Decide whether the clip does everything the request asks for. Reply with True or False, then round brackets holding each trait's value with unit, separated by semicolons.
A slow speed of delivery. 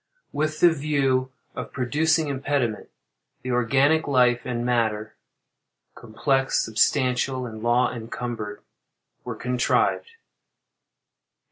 True (95 wpm)